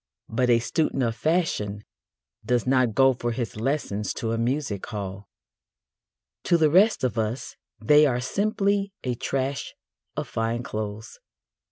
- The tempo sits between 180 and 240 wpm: No, average, 145 wpm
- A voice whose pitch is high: No, low, 125 Hz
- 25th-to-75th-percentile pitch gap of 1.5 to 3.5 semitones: No, average, 4.9 semitones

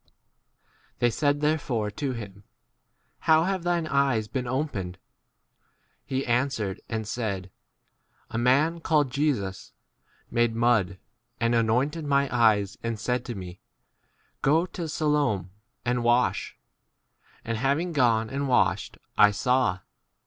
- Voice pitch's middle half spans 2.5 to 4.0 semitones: No, average, 4.6 semitones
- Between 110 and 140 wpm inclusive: Yes, slow, 135 wpm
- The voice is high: No, low, 125 Hz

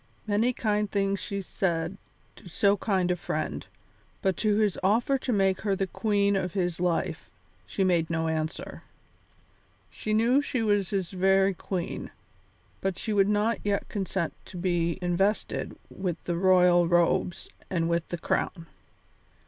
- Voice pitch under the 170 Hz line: No, high, 190 Hz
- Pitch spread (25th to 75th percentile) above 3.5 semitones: No, average, 2.8 semitones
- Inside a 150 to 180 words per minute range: Yes, average, 155 wpm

